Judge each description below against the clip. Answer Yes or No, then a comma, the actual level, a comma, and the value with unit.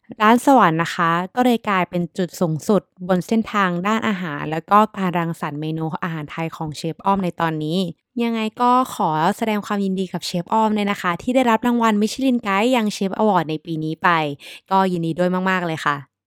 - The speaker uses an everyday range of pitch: Yes, average, 4.6 semitones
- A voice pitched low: No, medium, 185 Hz